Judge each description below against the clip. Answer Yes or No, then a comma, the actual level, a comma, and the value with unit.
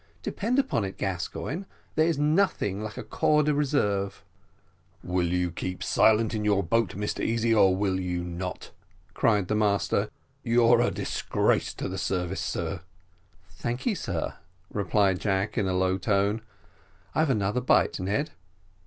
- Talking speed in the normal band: Yes, average, 155 wpm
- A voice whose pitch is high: No, low, 100 Hz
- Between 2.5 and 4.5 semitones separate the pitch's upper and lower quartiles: Yes, average, 4.1 semitones